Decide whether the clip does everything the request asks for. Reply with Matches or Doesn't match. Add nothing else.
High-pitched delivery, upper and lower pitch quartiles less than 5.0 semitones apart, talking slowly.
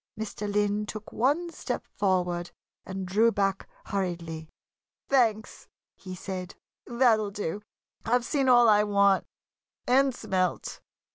Matches